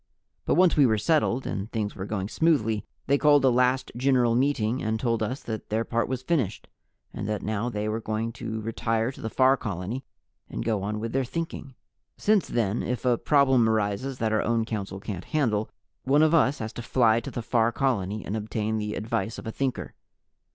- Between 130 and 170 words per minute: No, fast, 205 wpm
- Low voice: Yes, low, 115 Hz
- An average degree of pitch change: Yes, average, 3.4 semitones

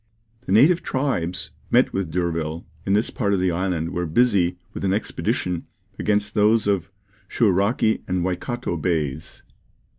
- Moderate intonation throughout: Yes, average, 3.5 semitones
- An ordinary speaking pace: Yes, average, 150 wpm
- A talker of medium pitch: No, very low, 95 Hz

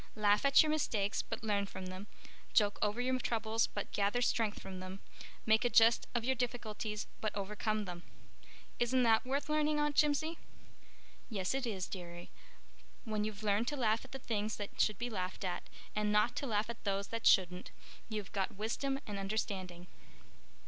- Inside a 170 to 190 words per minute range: Yes, average, 180 wpm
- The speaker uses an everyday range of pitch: Yes, average, 3.3 semitones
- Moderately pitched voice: No, high, 215 Hz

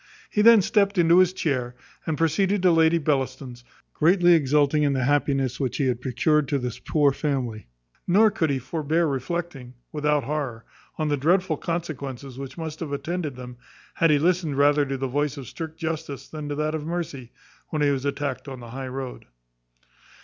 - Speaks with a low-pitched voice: No, medium, 145 Hz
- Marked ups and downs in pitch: No, average, 3.5 semitones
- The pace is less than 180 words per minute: No, average, 185 wpm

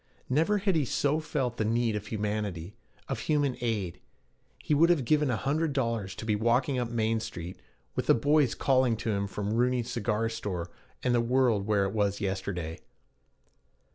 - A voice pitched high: No, low, 115 Hz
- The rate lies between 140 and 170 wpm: No, average, 180 wpm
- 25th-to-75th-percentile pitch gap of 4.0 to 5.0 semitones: Yes, average, 4.3 semitones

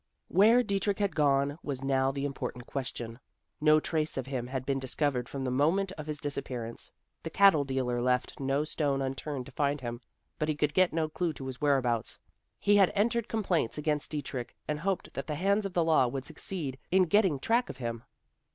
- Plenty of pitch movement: No, average, 4.5 semitones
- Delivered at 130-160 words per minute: No, average, 200 wpm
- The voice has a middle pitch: Yes, medium, 145 Hz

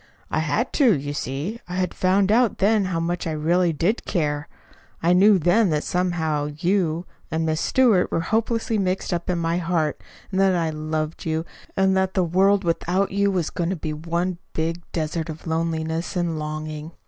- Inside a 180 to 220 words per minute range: Yes, average, 190 wpm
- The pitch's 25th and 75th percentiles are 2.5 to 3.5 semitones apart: Yes, average, 3.0 semitones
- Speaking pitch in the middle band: Yes, medium, 170 Hz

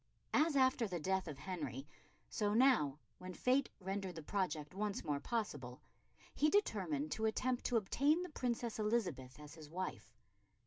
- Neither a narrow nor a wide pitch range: No, wide, 7.8 semitones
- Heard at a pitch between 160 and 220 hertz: Yes, high, 190 Hz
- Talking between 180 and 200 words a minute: No, average, 155 wpm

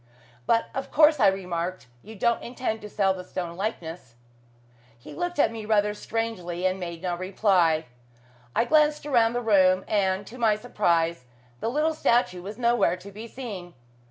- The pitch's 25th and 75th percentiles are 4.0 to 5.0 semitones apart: Yes, average, 4.4 semitones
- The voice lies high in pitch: Yes, high, 205 Hz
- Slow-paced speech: No, average, 170 wpm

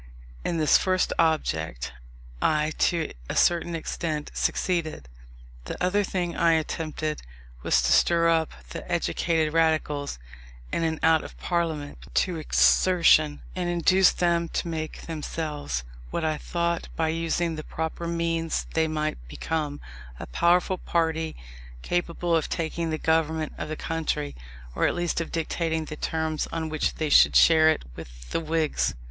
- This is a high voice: No, medium, 160 Hz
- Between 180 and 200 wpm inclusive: No, average, 150 wpm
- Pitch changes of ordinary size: No, narrow, 1.5 semitones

